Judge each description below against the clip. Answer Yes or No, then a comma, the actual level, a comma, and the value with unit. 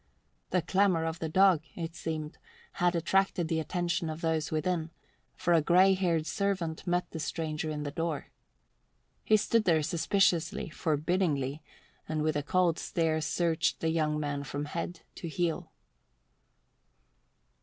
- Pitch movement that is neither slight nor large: No, narrow, 2.2 semitones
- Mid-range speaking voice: Yes, medium, 165 Hz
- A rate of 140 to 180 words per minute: Yes, average, 145 wpm